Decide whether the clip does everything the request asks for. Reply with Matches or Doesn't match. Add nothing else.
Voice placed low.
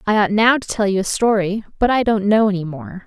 Doesn't match